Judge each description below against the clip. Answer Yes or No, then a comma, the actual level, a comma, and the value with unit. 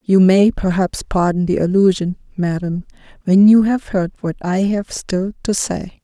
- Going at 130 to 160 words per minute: No, average, 170 wpm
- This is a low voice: No, high, 190 Hz